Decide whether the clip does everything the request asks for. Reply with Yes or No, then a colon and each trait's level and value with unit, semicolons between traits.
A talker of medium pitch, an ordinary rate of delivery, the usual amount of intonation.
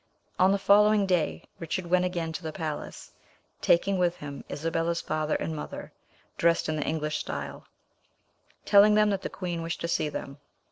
Yes: medium, 170 Hz; average, 175 wpm; average, 3.1 semitones